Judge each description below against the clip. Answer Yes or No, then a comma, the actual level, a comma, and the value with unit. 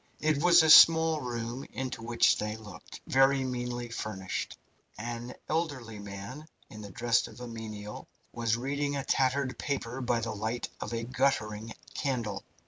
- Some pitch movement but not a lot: Yes, average, 3.3 semitones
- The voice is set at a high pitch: No, low, 120 Hz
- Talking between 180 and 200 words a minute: No, average, 155 wpm